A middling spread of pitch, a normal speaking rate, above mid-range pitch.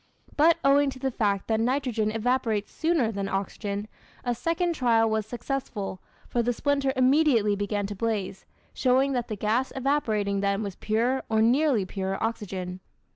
Yes: average, 4.5 semitones; average, 160 wpm; high, 225 Hz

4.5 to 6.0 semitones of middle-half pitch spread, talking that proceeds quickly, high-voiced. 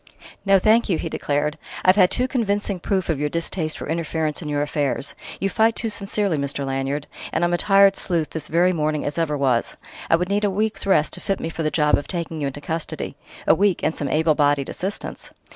No: average, 4.8 semitones; fast, 230 wpm; medium, 165 Hz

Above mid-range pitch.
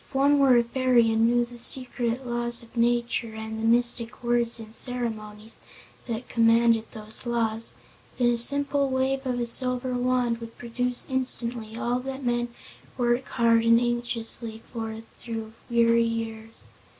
Yes: high, 235 Hz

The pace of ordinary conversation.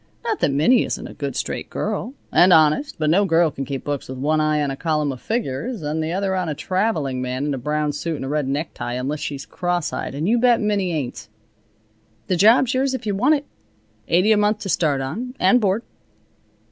No: fast, 225 wpm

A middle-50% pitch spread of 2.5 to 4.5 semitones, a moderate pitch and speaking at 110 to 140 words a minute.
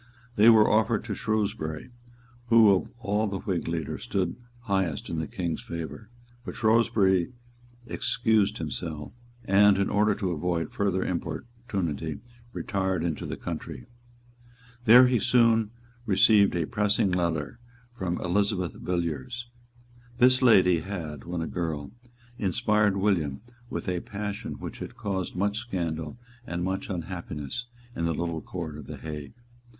No: average, 4.2 semitones; very low, 95 Hz; slow, 135 wpm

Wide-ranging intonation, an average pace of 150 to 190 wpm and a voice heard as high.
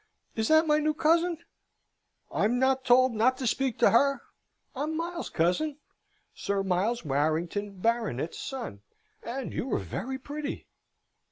No: wide, 6.3 semitones; average, 140 wpm; very high, 255 Hz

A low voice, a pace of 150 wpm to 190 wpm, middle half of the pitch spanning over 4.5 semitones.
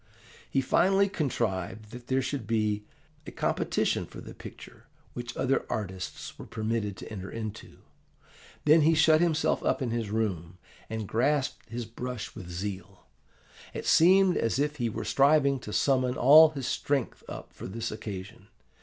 Yes: low, 120 Hz; average, 160 wpm; average, 5.1 semitones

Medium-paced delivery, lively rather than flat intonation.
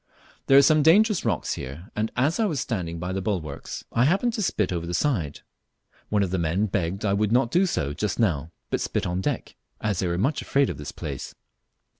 No: fast, 225 wpm; wide, 8.0 semitones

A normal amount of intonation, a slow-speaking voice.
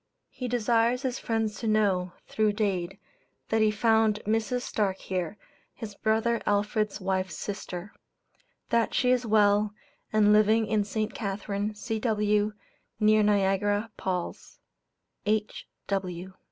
No: narrow, 1.5 semitones; slow, 120 wpm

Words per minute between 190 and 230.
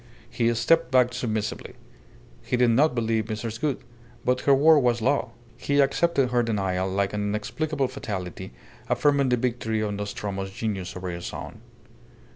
No: average, 155 wpm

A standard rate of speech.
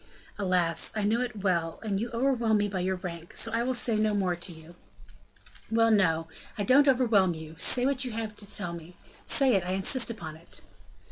No: fast, 210 wpm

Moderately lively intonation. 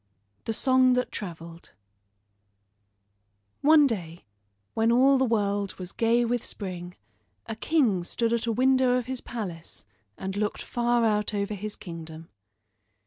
Yes: average, 4.6 semitones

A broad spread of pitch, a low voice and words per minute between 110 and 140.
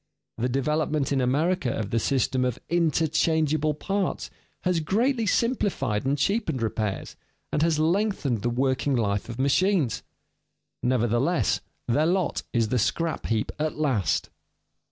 No: wide, 5.7 semitones; medium, 145 Hz; slow, 135 wpm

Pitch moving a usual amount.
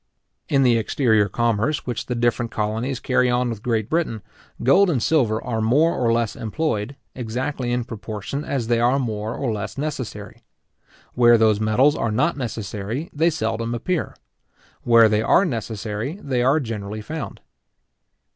Yes: average, 3.7 semitones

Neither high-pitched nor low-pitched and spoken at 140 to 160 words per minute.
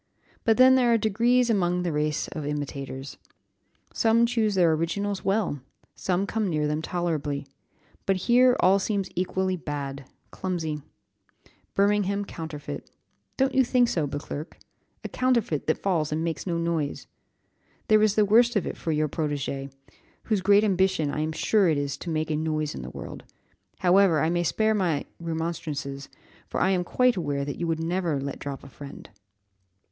No: medium, 170 Hz; average, 170 wpm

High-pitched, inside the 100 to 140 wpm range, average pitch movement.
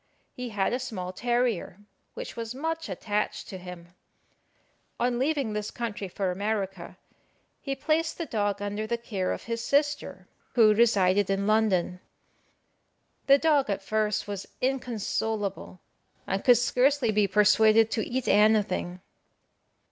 Yes: high, 215 Hz; slow, 135 wpm; average, 3.7 semitones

